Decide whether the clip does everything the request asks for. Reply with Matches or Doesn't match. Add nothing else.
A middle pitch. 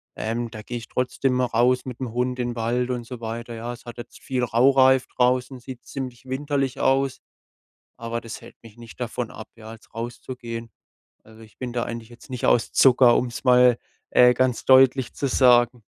Doesn't match